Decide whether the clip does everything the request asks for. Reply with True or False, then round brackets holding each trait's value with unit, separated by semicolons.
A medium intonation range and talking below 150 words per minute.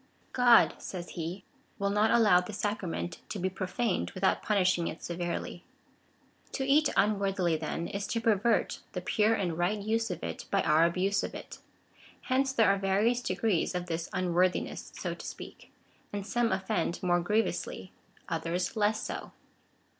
False (3.7 semitones; 170 wpm)